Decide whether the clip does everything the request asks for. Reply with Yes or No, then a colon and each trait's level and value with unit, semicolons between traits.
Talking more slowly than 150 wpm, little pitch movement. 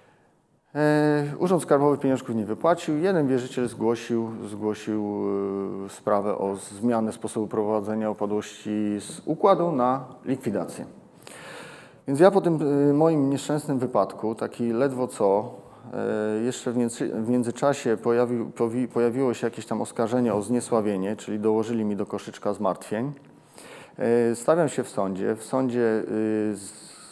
No: average, 115 wpm; average, 4.0 semitones